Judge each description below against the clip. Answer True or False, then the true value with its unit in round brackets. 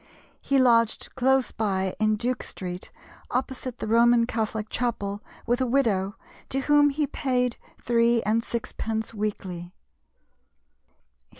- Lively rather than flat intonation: False (3.0 semitones)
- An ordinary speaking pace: False (120 wpm)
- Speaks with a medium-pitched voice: False (230 Hz)